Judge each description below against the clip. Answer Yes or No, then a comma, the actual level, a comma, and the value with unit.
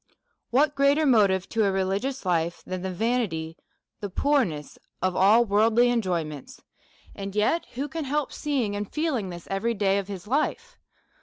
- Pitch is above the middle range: Yes, high, 210 Hz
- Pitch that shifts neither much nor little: No, wide, 6.0 semitones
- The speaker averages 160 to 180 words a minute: Yes, average, 165 wpm